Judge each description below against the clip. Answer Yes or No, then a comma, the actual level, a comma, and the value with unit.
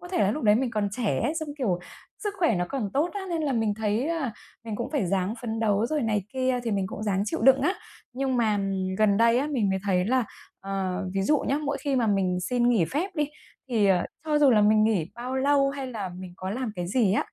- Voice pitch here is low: No, high, 225 Hz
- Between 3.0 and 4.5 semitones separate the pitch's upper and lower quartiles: No, average, 5.2 semitones